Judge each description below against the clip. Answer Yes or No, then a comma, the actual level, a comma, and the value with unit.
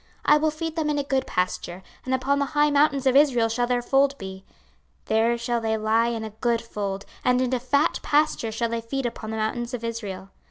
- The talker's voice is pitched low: No, high, 240 Hz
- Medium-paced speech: No, fast, 235 wpm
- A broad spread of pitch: No, average, 3.9 semitones